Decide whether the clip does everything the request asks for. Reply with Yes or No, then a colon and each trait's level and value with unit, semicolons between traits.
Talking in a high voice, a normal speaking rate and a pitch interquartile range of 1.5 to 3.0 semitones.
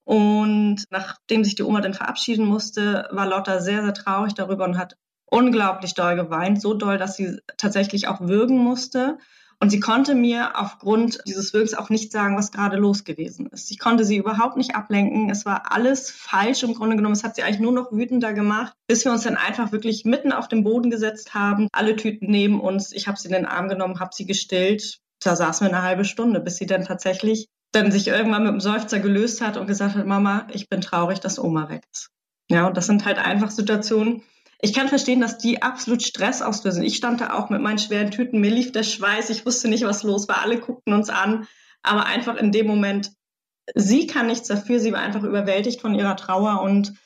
No: high, 210 Hz; fast, 220 wpm; narrow, 2.5 semitones